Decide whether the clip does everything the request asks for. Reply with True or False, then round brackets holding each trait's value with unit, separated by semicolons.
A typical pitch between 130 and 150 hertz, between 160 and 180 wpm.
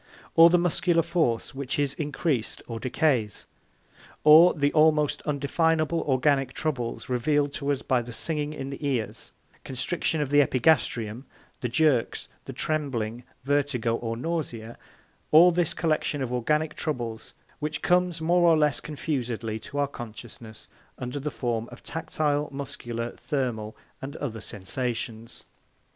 False (140 Hz; 140 wpm)